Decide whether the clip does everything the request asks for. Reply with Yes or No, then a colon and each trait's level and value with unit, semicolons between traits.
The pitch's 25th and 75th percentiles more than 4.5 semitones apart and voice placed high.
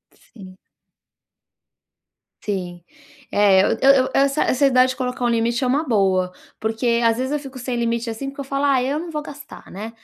No: average, 3.7 semitones; very high, 250 Hz